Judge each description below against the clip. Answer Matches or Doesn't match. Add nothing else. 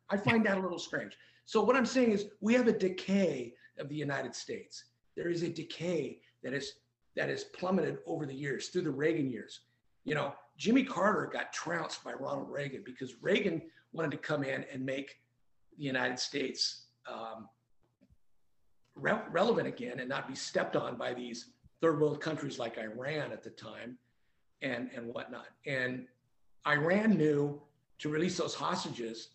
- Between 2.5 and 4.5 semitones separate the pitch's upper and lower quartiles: Doesn't match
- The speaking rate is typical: Matches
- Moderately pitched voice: Matches